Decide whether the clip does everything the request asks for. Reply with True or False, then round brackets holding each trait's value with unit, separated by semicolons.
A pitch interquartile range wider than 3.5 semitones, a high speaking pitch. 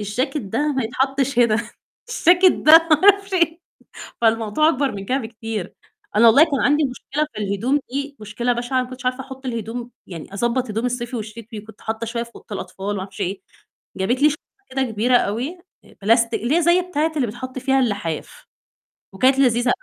True (4.0 semitones; 245 Hz)